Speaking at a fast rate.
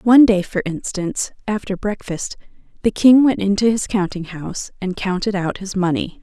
No: average, 175 wpm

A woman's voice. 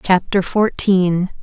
Yes: female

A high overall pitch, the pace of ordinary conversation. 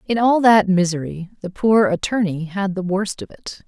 Yes: high, 195 Hz; average, 195 wpm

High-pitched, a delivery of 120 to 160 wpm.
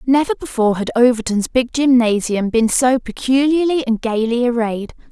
Yes: high, 240 Hz; average, 140 wpm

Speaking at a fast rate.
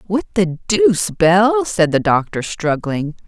No: average, 145 wpm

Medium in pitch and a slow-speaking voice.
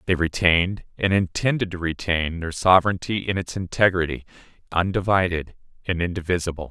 No: very low, 90 Hz; slow, 115 wpm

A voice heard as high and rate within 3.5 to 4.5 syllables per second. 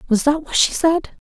No: very high, 290 Hz; 5.0 syllables/s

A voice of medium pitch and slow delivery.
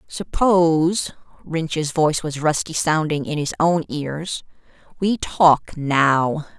Yes: medium, 160 Hz; slow, 120 wpm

